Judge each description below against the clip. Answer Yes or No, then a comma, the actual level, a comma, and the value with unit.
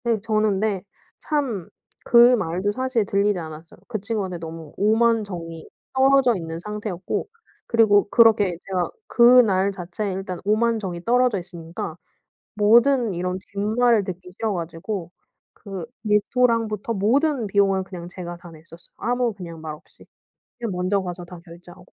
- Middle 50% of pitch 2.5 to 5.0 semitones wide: Yes, average, 4.3 semitones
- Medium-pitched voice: No, high, 200 Hz